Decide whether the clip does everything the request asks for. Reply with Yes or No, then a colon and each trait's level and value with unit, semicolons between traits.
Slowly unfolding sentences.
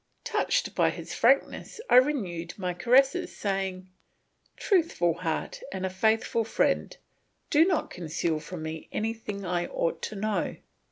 Yes: slow, 130 wpm